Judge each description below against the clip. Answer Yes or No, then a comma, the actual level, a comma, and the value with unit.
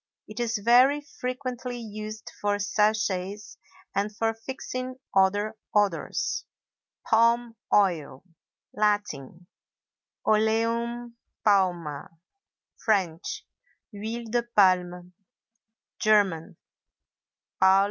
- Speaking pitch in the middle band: No, high, 215 Hz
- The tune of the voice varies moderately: Yes, average, 3.4 semitones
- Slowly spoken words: Yes, slow, 65 wpm